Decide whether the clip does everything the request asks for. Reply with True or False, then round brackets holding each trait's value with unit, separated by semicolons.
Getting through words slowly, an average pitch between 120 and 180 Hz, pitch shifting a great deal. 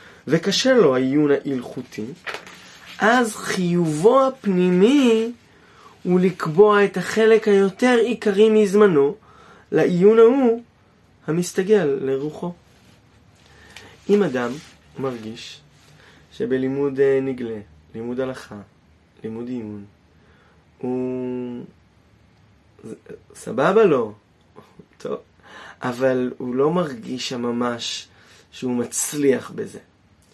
True (75 wpm; 135 Hz; 8.7 semitones)